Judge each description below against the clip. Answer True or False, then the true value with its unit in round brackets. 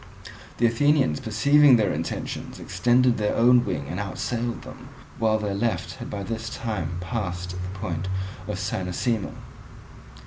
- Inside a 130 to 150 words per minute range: True (140 wpm)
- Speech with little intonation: False (4.2 semitones)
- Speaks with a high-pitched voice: False (110 Hz)